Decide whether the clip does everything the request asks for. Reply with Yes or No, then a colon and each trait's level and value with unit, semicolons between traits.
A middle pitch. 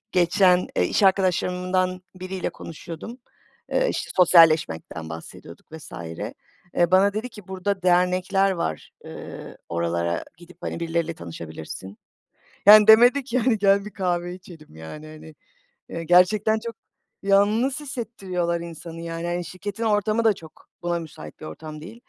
Yes: medium, 180 Hz